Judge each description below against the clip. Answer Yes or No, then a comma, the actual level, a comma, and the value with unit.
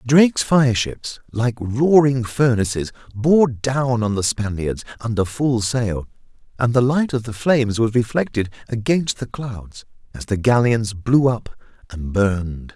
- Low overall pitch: Yes, low, 120 Hz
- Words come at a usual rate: Yes, average, 150 wpm